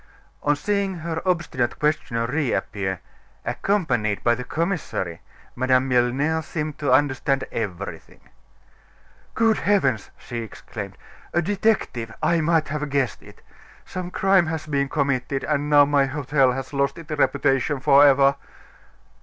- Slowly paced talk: Yes, slow, 130 wpm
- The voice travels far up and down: No, average, 3.9 semitones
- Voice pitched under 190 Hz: Yes, medium, 140 Hz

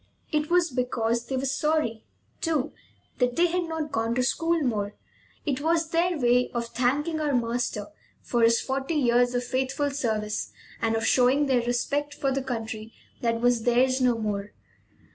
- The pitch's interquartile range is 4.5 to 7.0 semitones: No, average, 4.0 semitones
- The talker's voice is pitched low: No, very high, 250 Hz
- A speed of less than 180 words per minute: Yes, average, 170 wpm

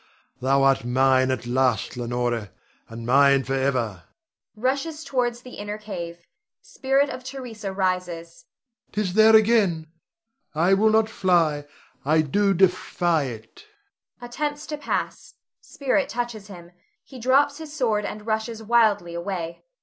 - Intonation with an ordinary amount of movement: No, wide, 8.8 semitones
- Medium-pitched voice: No, high, 195 Hz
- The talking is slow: Yes, slow, 130 wpm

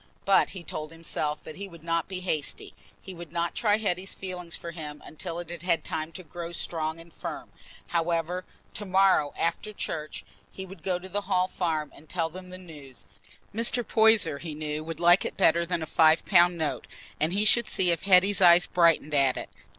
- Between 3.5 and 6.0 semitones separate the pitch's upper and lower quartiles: No, average, 2.7 semitones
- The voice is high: No, medium, 170 Hz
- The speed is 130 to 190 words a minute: No, average, 200 wpm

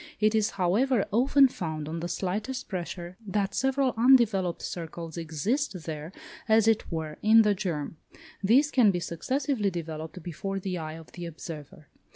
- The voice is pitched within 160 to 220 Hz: Yes, high, 190 Hz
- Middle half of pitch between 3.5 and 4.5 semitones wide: No, average, 5.3 semitones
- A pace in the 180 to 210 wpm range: No, average, 160 wpm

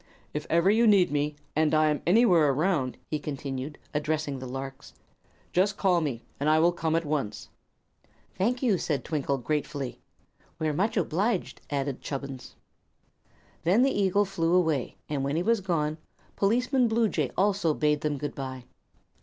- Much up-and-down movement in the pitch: No, average, 5.0 semitones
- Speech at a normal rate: Yes, average, 160 wpm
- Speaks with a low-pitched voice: No, medium, 155 Hz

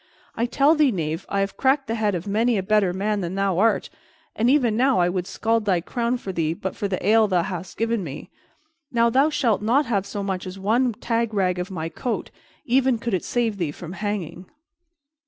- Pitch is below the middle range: No, high, 210 Hz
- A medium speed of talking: No, fast, 220 wpm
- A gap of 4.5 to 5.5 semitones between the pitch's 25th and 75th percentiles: No, average, 4.1 semitones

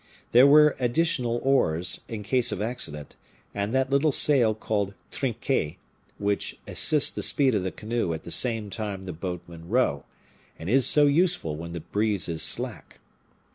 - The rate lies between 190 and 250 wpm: No, average, 165 wpm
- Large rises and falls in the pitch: Yes, wide, 6.4 semitones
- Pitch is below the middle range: Yes, low, 110 Hz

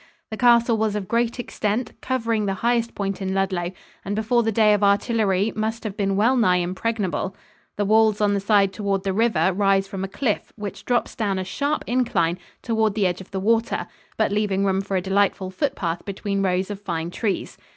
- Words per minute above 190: Yes, fast, 205 wpm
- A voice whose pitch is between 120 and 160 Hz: No, high, 205 Hz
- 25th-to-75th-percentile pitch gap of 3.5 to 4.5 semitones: No, average, 2.7 semitones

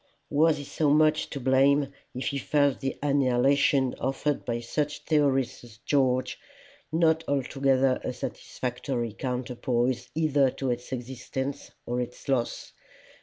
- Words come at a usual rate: No, slow, 130 wpm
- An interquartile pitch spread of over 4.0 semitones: No, narrow, 2.4 semitones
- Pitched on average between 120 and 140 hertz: Yes, low, 135 Hz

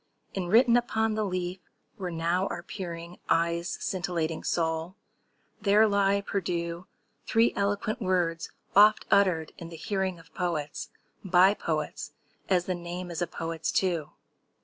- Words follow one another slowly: Yes, slow, 130 wpm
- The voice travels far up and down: No, average, 3.0 semitones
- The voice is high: No, medium, 180 Hz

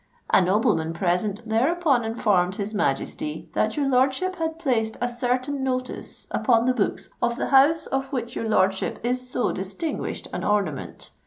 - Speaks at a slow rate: No, average, 160 wpm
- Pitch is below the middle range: No, high, 235 Hz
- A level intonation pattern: No, average, 4.5 semitones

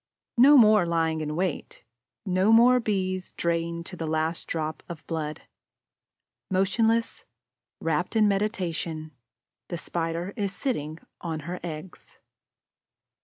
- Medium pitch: Yes, medium, 175 Hz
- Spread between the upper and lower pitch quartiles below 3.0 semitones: No, average, 3.9 semitones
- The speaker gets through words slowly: Yes, slow, 120 wpm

